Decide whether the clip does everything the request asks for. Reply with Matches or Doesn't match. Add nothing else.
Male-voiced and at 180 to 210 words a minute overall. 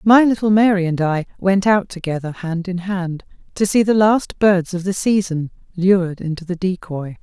Doesn't match